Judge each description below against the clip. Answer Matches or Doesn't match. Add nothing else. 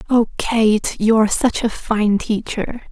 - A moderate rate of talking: Matches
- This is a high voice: Matches